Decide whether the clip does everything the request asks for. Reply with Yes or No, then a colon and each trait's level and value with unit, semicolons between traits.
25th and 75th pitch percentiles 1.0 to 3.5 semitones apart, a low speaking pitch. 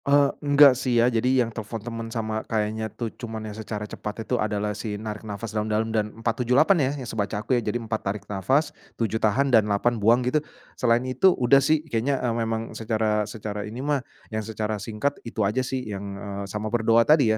Yes: average, 2.8 semitones; low, 110 Hz